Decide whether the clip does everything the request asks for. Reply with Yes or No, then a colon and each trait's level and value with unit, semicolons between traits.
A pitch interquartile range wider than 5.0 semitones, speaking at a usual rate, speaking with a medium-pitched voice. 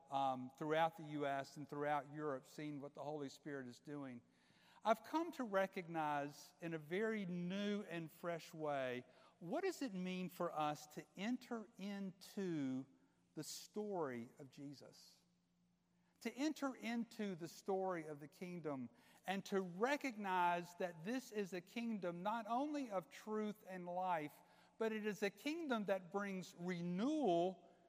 Yes: wide, 5.5 semitones; average, 145 wpm; medium, 180 Hz